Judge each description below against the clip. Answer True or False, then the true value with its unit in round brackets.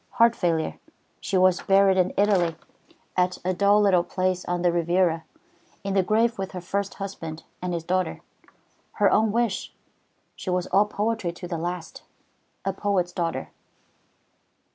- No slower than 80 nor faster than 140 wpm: False (155 wpm)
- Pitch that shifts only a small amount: True (2.2 semitones)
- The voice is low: False (185 Hz)